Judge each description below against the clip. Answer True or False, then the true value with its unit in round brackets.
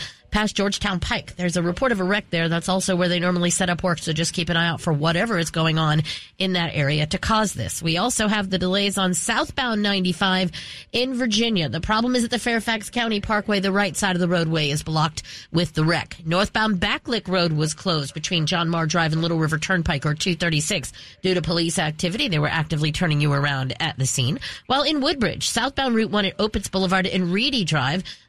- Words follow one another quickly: True (220 wpm)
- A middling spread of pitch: True (4.2 semitones)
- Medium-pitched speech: True (180 Hz)